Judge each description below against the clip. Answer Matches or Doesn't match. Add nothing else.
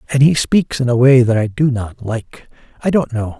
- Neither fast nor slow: Doesn't match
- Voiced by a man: Matches